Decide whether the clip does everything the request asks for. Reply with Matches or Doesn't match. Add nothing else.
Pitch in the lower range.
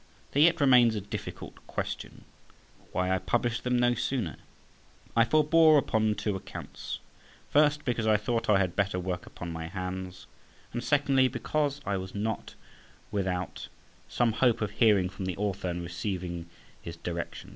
Matches